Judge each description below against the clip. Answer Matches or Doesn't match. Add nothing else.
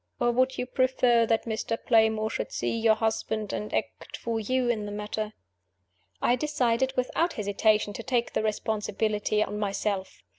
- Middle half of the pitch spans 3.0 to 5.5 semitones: Doesn't match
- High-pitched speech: Matches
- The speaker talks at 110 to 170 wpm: Matches